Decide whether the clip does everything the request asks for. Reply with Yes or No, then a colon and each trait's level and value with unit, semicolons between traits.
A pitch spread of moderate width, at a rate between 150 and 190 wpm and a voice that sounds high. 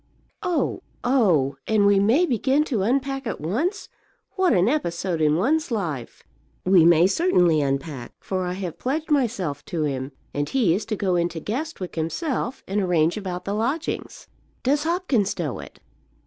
No: wide, 8.1 semitones; average, 160 wpm; high, 200 Hz